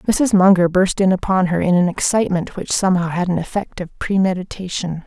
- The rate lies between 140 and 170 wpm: No, average, 190 wpm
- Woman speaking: Yes, female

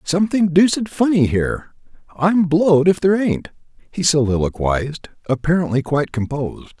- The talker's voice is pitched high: No, medium, 160 Hz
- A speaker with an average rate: No, slow, 125 wpm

